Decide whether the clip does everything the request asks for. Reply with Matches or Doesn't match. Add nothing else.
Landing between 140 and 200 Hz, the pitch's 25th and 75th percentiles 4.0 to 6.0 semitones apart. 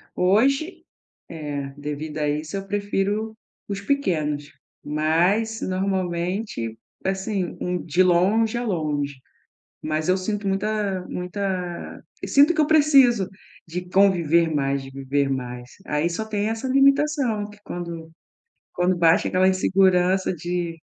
Matches